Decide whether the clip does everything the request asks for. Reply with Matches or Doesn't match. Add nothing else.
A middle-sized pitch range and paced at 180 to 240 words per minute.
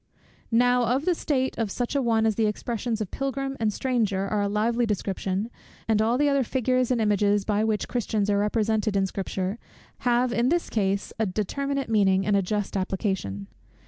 Matches